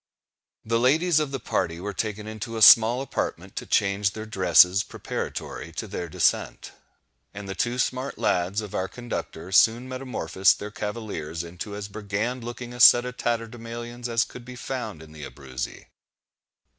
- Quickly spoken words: No, average, 165 wpm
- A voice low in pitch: Yes, low, 110 Hz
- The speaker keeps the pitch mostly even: No, average, 3.9 semitones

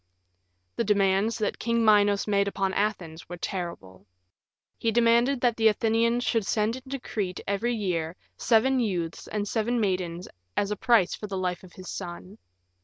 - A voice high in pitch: Yes, high, 205 Hz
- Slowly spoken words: No, average, 165 wpm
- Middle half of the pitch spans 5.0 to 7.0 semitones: No, average, 3.8 semitones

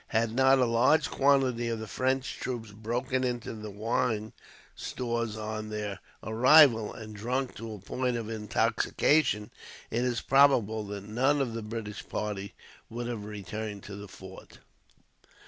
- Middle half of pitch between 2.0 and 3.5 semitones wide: Yes, average, 3.0 semitones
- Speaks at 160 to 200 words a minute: No, average, 150 wpm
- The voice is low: Yes, low, 115 Hz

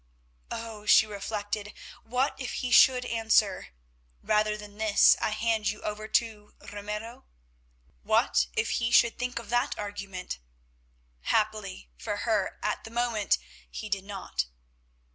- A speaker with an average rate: No, slow, 130 wpm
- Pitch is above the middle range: Yes, high, 215 Hz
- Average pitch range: No, narrow, 2.1 semitones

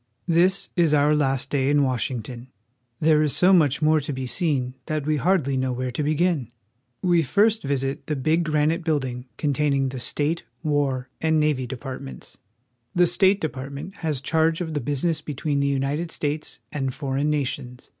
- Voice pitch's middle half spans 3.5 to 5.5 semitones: No, average, 3.1 semitones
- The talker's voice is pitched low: No, medium, 145 Hz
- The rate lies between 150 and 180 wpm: Yes, average, 175 wpm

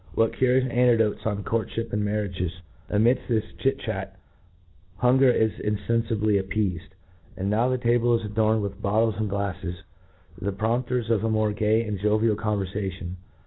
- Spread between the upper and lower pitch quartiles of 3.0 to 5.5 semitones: No, narrow, 2.4 semitones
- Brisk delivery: No, average, 155 wpm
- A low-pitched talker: Yes, low, 105 Hz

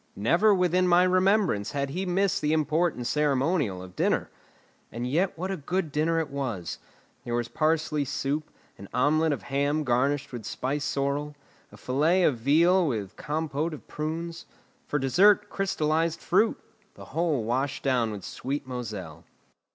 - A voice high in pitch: No, medium, 150 Hz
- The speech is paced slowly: No, average, 155 wpm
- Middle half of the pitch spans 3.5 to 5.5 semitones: Yes, average, 4.6 semitones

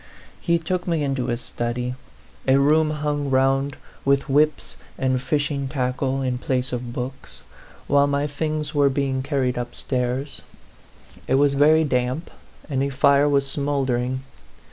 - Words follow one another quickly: No, average, 145 wpm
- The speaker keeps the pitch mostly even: Yes, narrow, 2.0 semitones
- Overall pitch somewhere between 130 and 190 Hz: Yes, medium, 140 Hz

